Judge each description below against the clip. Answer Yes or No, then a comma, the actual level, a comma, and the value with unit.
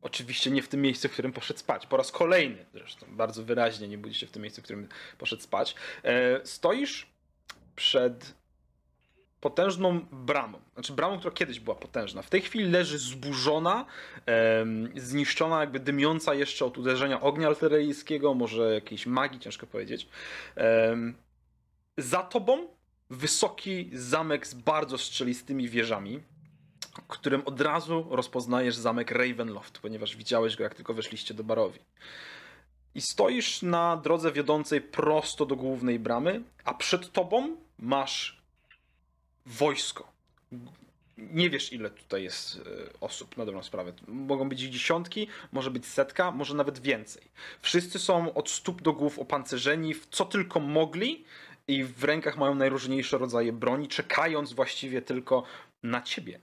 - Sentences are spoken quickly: No, average, 140 wpm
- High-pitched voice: No, medium, 140 Hz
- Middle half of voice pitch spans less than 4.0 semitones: No, average, 4.3 semitones